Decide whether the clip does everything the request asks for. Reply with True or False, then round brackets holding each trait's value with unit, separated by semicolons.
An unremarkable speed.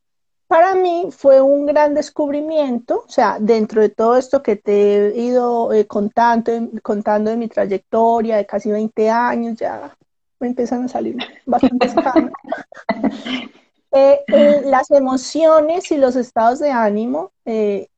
True (140 wpm)